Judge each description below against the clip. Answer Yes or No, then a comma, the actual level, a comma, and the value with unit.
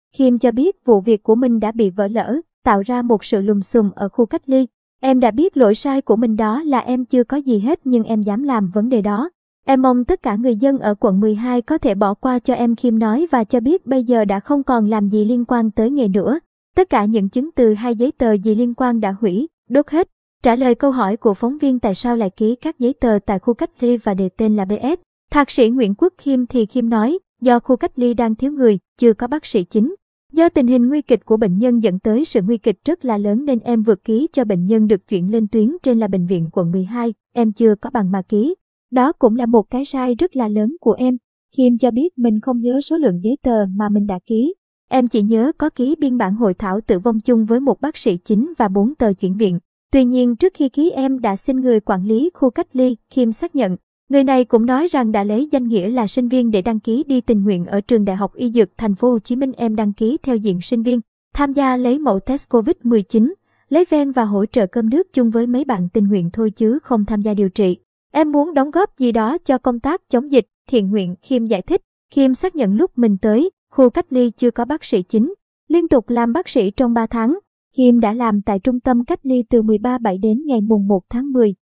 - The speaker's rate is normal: No, fast, 260 wpm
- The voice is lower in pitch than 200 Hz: No, high, 240 Hz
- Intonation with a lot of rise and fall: No, average, 3.4 semitones